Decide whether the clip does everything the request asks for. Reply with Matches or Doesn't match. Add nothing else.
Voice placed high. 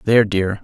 Doesn't match